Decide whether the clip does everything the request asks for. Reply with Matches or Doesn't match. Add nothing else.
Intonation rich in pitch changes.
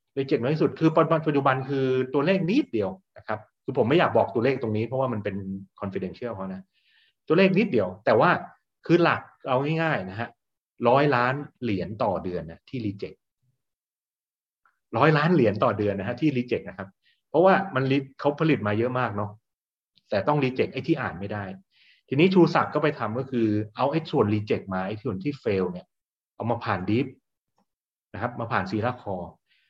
Matches